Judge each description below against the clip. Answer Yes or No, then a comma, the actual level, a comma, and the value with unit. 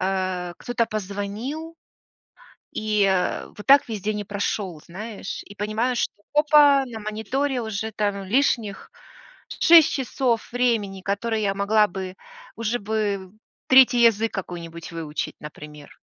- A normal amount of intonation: Yes, average, 3.6 semitones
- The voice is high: Yes, high, 210 Hz